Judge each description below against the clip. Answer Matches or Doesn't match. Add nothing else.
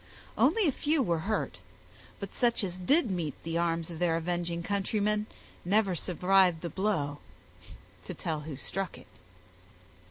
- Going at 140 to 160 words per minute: Matches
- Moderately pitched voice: Matches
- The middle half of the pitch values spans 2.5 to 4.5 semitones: Matches